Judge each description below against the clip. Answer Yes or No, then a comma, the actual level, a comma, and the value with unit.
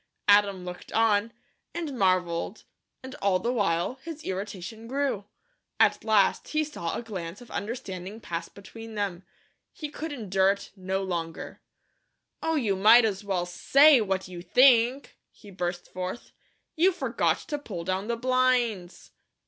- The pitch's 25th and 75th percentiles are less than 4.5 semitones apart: No, average, 4.9 semitones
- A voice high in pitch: Yes, high, 205 Hz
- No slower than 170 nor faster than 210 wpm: No, average, 150 wpm